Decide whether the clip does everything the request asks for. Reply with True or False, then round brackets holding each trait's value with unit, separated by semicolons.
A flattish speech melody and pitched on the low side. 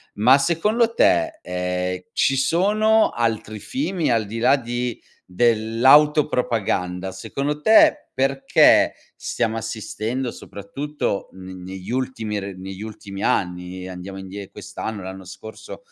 False (6.6 semitones; 110 Hz)